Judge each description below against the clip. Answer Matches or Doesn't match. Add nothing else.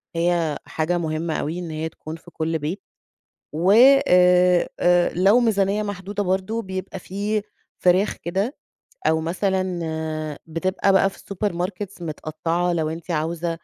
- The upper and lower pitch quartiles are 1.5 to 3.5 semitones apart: Matches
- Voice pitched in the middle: Matches